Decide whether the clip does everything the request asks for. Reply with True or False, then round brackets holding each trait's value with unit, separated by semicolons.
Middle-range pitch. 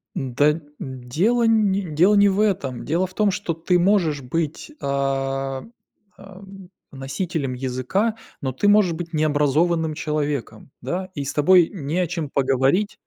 True (160 Hz)